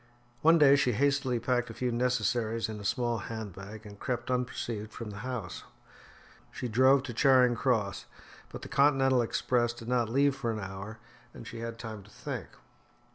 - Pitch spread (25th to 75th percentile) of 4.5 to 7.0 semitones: No, average, 2.7 semitones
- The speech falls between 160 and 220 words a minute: Yes, average, 185 wpm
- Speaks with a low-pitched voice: Yes, low, 120 Hz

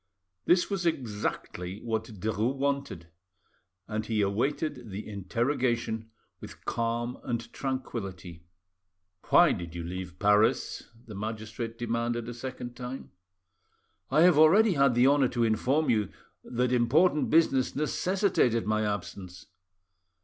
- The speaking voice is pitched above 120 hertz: No, low, 115 Hz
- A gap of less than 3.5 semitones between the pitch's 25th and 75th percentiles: No, average, 4.2 semitones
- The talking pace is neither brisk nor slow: No, slow, 120 wpm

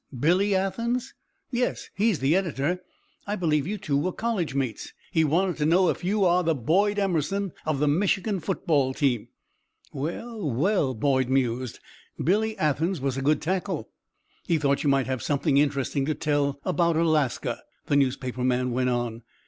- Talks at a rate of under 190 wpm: Yes, average, 170 wpm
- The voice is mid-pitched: Yes, medium, 155 Hz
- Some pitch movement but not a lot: No, wide, 5.7 semitones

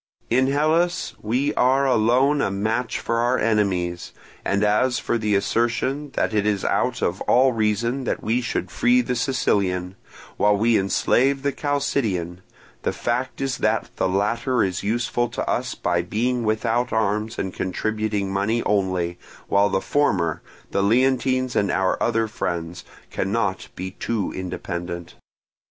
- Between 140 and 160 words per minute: Yes, average, 150 wpm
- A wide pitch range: No, average, 4.3 semitones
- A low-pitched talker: Yes, low, 110 Hz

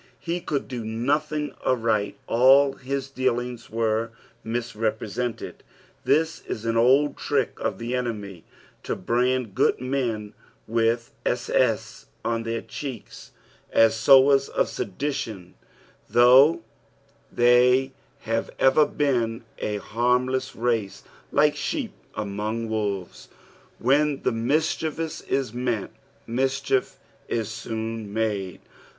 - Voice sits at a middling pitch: No, low, 120 Hz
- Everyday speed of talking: No, slow, 110 wpm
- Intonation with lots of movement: No, average, 3.1 semitones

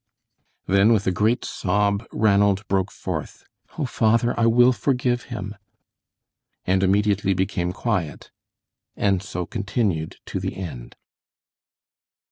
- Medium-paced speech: No, slow, 115 wpm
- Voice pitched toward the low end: Yes, low, 100 Hz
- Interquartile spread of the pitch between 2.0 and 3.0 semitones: No, average, 3.4 semitones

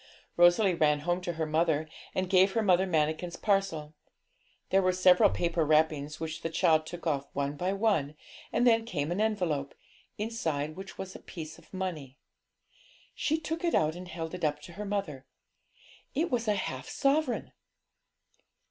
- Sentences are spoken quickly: No, average, 170 wpm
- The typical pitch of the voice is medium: Yes, medium, 175 Hz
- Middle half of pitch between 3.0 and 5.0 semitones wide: Yes, average, 4.1 semitones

